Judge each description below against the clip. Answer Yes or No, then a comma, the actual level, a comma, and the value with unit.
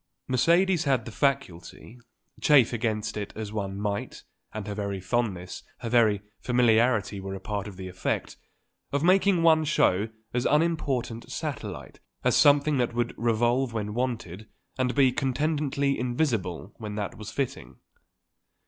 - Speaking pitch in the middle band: No, low, 120 Hz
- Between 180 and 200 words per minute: No, average, 150 wpm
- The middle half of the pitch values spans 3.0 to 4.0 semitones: No, average, 4.9 semitones